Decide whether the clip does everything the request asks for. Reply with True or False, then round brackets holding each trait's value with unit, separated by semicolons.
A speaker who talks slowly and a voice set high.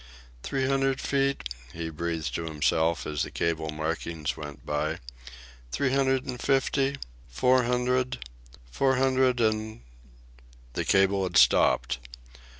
False (130 wpm; 100 Hz)